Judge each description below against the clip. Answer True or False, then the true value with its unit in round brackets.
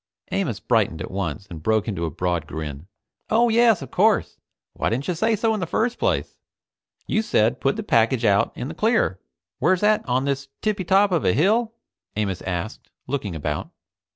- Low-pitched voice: True (130 Hz)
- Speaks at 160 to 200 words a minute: True (190 wpm)